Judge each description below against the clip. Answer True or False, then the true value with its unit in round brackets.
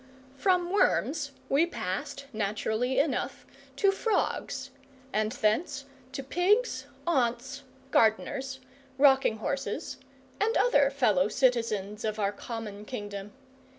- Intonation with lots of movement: False (5.0 semitones)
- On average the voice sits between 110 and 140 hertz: False (260 Hz)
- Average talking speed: False (105 wpm)